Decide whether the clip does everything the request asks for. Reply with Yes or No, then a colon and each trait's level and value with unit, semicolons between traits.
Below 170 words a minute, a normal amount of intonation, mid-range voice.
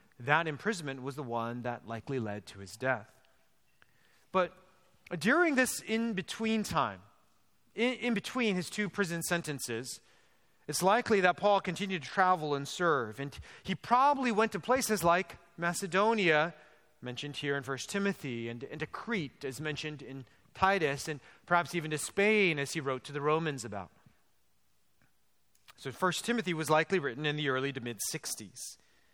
No: average, 160 wpm; wide, 6.6 semitones; medium, 155 Hz